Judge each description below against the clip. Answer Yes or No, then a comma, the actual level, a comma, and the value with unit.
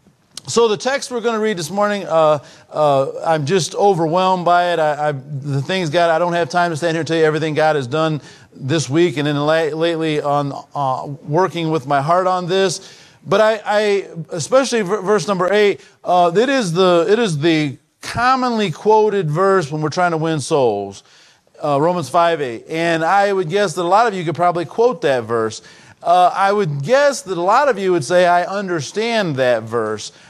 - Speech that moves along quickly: Yes, fast, 210 wpm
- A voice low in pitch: No, medium, 175 Hz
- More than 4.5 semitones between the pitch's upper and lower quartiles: No, average, 4.2 semitones